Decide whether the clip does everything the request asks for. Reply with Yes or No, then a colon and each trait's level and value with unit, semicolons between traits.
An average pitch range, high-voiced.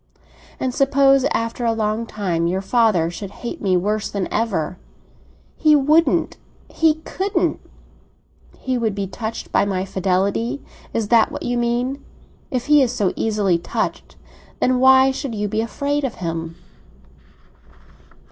Yes: average, 5.0 semitones; high, 225 Hz